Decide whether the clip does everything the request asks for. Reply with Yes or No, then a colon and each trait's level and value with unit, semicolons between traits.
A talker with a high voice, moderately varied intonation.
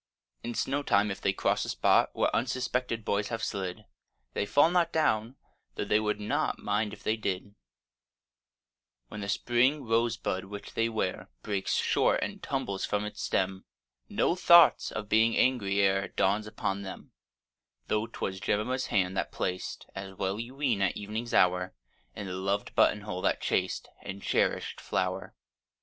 No: low, 105 Hz; average, 3.2 semitones